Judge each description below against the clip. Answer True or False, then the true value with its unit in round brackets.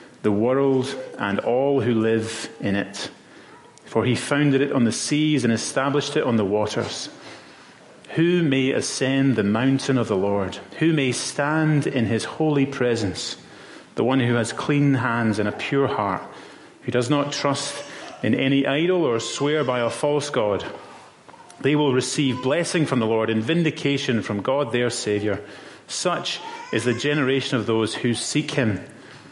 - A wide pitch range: False (4.1 semitones)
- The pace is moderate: True (165 wpm)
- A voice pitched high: False (130 Hz)